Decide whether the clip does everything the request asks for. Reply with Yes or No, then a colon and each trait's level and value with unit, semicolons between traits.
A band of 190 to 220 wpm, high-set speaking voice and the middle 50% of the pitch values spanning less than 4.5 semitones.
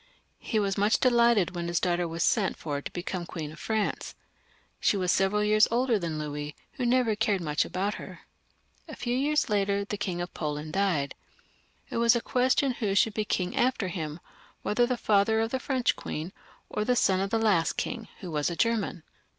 No: fast, 205 wpm; high, 200 Hz; average, 4.9 semitones